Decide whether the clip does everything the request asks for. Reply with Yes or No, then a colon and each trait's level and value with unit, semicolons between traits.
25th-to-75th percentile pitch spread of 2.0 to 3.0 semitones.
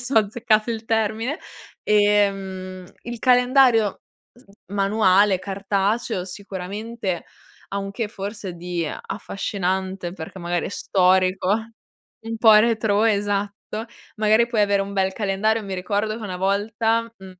Yes: narrow, 2.6 semitones